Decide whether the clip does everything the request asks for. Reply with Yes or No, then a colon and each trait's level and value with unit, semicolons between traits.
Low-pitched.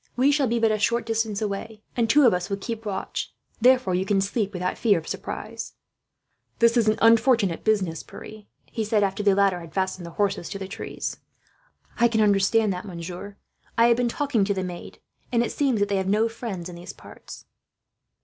No: high, 210 Hz